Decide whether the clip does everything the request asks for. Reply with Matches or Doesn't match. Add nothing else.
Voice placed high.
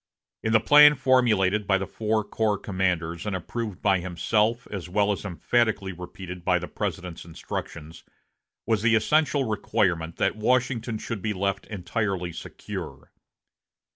Doesn't match